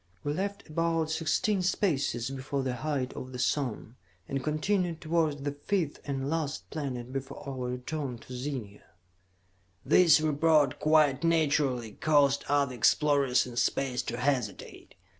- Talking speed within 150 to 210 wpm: No, average, 140 wpm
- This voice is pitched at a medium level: Yes, medium, 145 Hz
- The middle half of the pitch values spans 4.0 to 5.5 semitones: No, average, 3.4 semitones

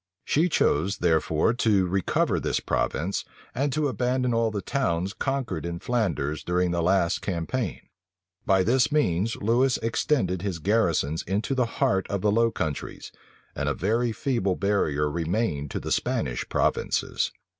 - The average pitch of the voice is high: No, low, 100 Hz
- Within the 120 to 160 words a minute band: Yes, average, 150 wpm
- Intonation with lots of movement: Yes, wide, 5.7 semitones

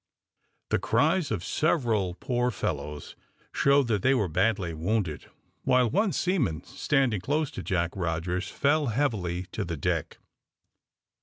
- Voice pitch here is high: No, low, 110 Hz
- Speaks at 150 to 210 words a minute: No, slow, 135 wpm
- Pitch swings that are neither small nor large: No, wide, 7.9 semitones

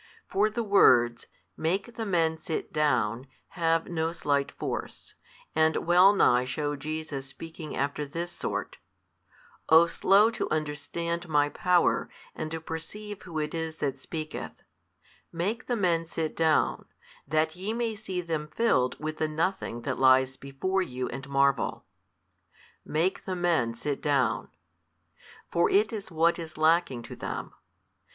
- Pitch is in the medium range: Yes, medium, 160 Hz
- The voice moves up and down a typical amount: Yes, average, 3.5 semitones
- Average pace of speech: Yes, average, 145 wpm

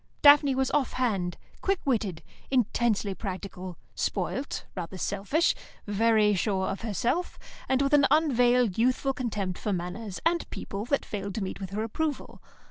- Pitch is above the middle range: Yes, high, 225 Hz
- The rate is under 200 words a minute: Yes, average, 150 wpm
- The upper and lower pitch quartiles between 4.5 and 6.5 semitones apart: Yes, wide, 5.4 semitones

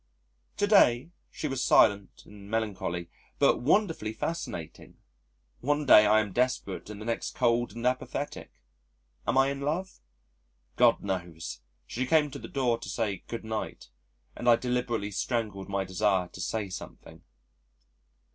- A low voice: Yes, low, 115 Hz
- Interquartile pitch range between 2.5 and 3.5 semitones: No, average, 4.4 semitones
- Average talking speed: Yes, average, 145 wpm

